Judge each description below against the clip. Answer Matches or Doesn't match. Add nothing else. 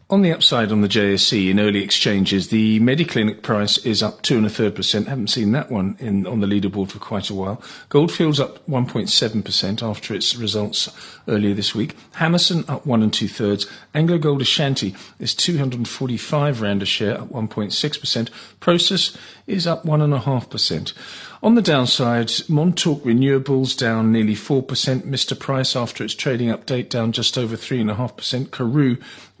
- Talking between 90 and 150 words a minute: Doesn't match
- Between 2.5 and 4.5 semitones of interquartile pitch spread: Doesn't match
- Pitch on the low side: Matches